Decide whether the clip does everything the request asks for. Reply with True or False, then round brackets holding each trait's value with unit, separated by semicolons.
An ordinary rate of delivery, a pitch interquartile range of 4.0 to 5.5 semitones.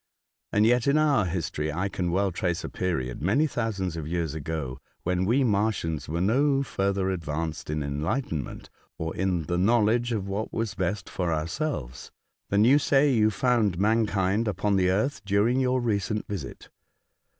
True (170 wpm; 5.2 semitones)